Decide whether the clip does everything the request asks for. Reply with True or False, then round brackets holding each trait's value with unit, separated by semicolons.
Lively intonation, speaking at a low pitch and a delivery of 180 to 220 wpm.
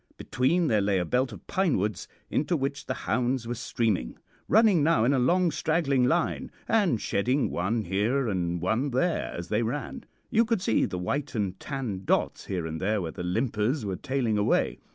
True (6.2 semitones; 120 Hz; 195 wpm)